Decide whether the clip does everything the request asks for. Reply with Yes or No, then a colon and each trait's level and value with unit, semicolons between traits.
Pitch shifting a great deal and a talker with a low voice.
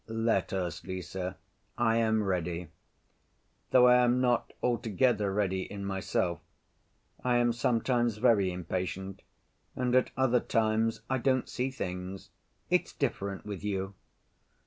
No: average, 4.2 semitones; low, 110 Hz